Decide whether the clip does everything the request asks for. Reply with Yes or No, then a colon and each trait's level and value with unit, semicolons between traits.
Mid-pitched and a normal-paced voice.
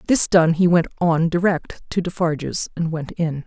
Yes: medium, 170 Hz; average, 190 wpm